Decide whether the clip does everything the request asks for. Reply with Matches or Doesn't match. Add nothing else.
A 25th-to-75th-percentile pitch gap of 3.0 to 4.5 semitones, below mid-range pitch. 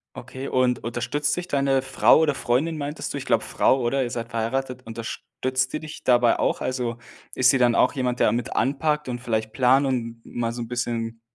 Doesn't match